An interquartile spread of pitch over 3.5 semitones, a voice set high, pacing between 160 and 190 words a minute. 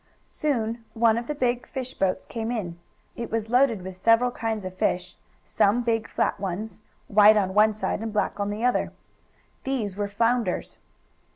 No: average, 2.9 semitones; high, 220 Hz; average, 175 wpm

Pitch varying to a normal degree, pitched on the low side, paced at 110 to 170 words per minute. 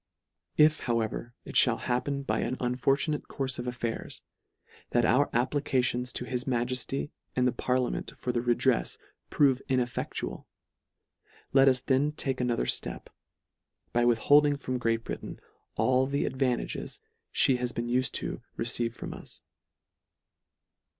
No: narrow, 1.8 semitones; low, 125 Hz; slow, 135 wpm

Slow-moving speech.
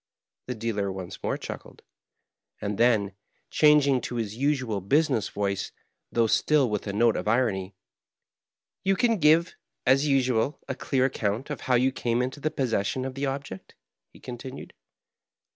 No: average, 160 wpm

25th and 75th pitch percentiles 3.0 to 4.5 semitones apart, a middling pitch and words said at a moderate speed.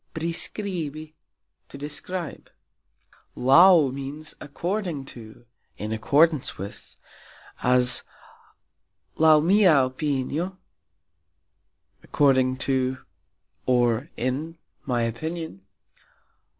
No: average, 4.2 semitones; medium, 145 Hz; slow, 70 wpm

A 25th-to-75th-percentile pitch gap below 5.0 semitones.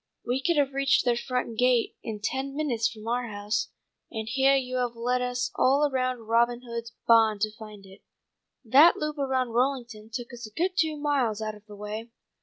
Yes: average, 3.2 semitones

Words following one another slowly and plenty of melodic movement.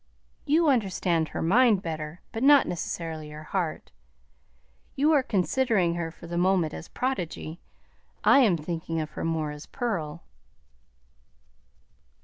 Yes: slow, 130 wpm; wide, 6.4 semitones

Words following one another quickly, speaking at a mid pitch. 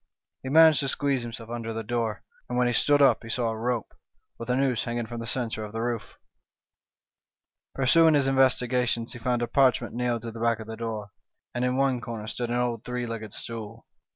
No: fast, 230 wpm; low, 120 Hz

